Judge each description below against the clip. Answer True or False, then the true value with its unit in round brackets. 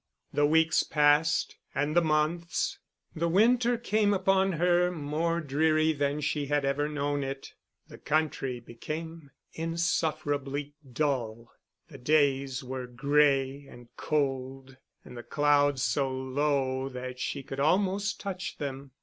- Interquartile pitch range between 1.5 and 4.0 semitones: True (3.2 semitones)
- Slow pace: True (130 wpm)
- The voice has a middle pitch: True (145 Hz)